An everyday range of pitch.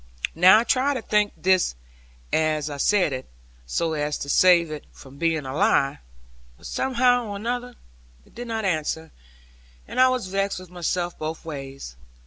No: wide, 6.1 semitones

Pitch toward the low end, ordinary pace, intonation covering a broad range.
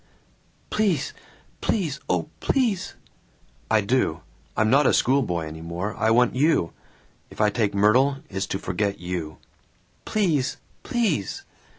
No: low, 115 Hz; slow, 125 wpm; wide, 7.2 semitones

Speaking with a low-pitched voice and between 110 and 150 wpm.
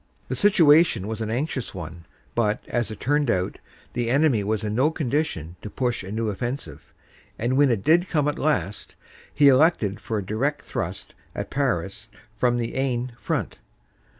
No: low, 120 Hz; average, 175 wpm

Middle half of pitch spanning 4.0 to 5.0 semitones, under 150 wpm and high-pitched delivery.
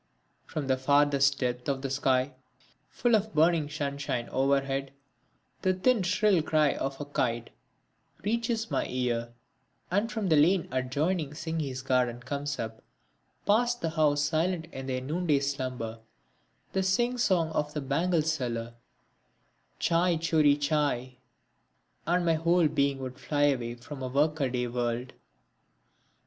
No: average, 4.3 semitones; average, 140 wpm; medium, 145 Hz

